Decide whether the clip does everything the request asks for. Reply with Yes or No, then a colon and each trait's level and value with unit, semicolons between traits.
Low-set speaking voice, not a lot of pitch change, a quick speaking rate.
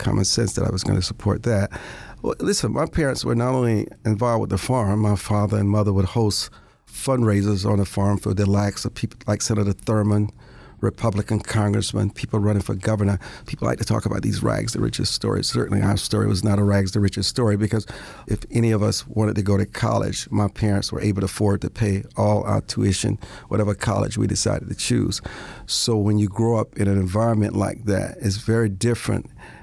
Yes: low, 105 Hz; narrow, 2.0 semitones; fast, 215 wpm